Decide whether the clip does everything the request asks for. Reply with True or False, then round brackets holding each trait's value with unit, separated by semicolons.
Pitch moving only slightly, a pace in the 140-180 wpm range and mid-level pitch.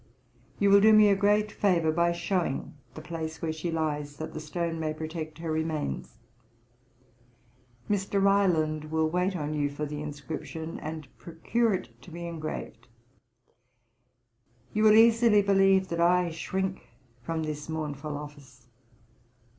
False (3.8 semitones; 145 wpm; 165 Hz)